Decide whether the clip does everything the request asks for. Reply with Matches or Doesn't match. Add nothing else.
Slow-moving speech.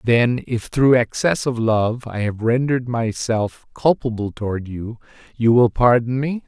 Doesn't match